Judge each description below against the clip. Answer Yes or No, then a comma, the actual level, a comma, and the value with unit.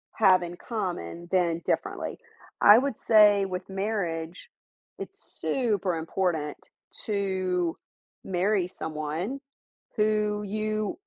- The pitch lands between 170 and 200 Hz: Yes, high, 190 Hz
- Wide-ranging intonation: No, average, 3.4 semitones